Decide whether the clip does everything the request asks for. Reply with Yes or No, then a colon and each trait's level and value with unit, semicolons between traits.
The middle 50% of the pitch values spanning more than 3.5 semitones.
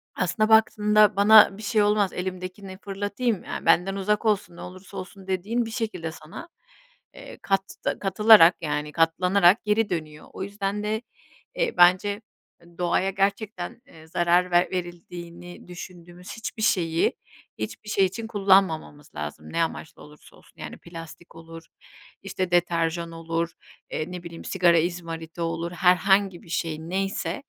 No: average, 3.2 semitones